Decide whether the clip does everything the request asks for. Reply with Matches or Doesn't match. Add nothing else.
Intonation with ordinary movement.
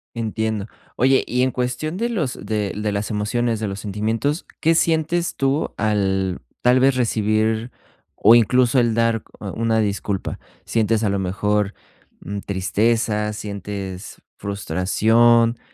Matches